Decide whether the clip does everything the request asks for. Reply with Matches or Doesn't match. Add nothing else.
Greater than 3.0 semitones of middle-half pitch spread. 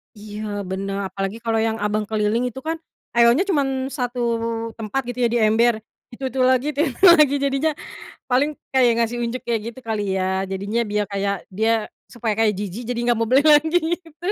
Matches